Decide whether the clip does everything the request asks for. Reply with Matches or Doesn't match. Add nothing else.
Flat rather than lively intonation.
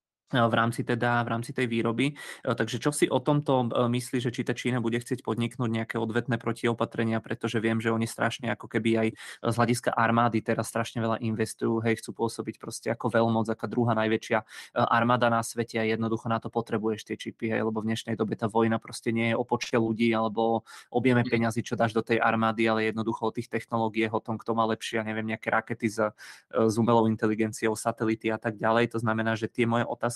Matches